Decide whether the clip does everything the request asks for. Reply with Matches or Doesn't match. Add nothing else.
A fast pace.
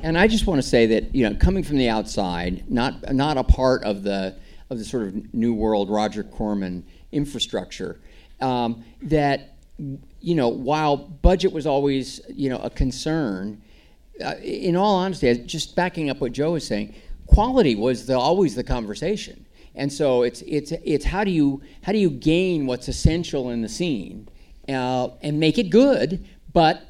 Doesn't match